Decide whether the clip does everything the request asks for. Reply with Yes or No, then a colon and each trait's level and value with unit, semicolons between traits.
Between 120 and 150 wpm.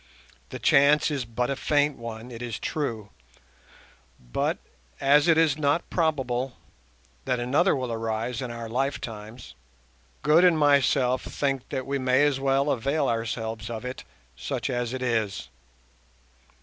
Yes: average, 145 wpm